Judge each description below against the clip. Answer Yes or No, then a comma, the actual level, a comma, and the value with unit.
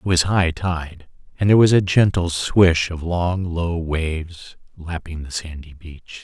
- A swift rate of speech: No, average, 175 wpm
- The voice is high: No, very low, 85 Hz